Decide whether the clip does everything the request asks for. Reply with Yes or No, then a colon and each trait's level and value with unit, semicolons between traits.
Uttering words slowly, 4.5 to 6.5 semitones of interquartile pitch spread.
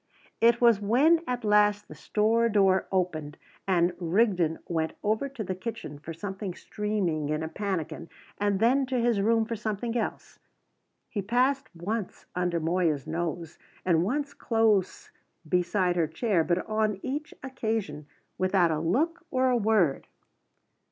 No: average, 150 wpm; average, 5.0 semitones